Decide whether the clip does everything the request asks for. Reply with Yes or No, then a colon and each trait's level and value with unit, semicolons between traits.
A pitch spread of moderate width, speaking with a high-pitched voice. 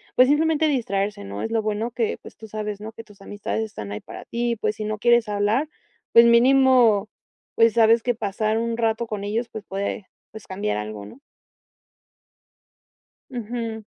No: narrow, 2.3 semitones; high, 220 Hz